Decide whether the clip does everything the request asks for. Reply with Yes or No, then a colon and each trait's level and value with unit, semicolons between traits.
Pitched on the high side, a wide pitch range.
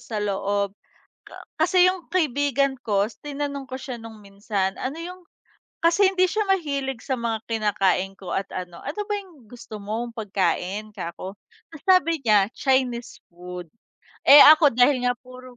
Yes: high, 245 Hz; wide, 6.1 semitones